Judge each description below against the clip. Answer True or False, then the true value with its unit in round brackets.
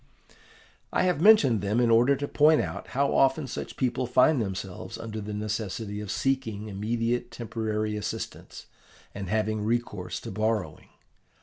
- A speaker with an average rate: True (145 wpm)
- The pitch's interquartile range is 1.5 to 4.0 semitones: True (3.3 semitones)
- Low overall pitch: True (115 Hz)